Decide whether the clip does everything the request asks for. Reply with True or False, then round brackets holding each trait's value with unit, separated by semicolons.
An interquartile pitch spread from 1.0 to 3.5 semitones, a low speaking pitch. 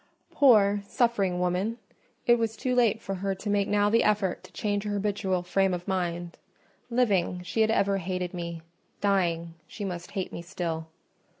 False (2.9 semitones; 195 Hz)